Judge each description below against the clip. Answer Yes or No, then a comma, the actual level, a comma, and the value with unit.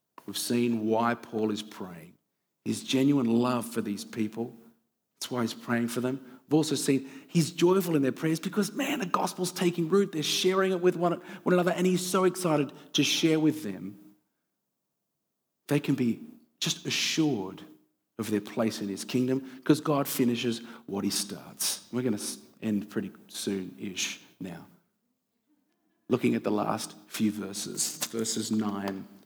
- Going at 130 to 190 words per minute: Yes, average, 165 wpm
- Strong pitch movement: Yes, wide, 7.7 semitones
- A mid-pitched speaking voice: No, low, 130 Hz